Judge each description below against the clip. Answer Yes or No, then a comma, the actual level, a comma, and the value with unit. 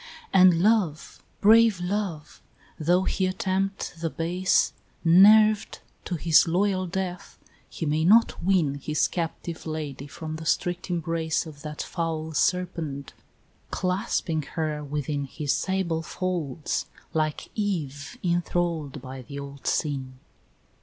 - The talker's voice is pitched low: No, medium, 165 Hz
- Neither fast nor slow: No, slow, 120 wpm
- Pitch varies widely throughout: No, average, 3.5 semitones